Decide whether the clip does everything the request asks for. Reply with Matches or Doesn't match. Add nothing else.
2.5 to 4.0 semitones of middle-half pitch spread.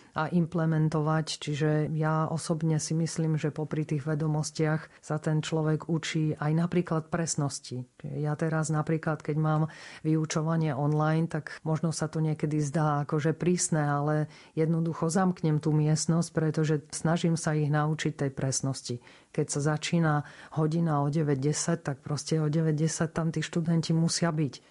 Doesn't match